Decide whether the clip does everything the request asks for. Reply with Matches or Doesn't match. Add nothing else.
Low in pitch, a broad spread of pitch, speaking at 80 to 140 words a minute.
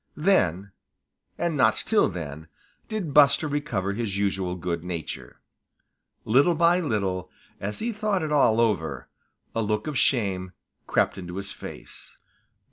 Matches